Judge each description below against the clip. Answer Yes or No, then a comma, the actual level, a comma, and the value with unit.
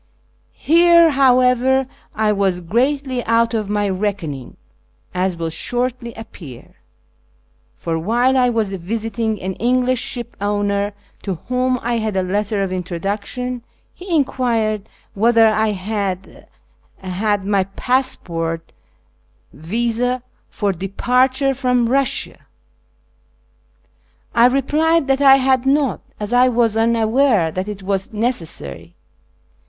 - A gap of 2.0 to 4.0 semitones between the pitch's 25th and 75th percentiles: No, average, 4.5 semitones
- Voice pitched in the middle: No, high, 225 Hz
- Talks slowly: Yes, slow, 115 wpm